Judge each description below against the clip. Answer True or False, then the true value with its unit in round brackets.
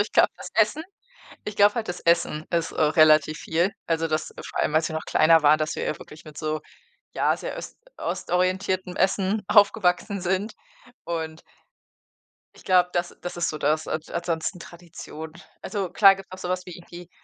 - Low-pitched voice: False (175 Hz)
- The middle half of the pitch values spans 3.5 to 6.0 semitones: False (2.9 semitones)